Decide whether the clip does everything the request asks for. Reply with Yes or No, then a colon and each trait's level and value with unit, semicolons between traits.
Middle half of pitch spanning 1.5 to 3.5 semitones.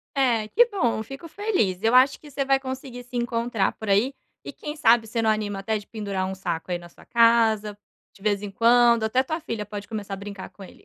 No: average, 3.9 semitones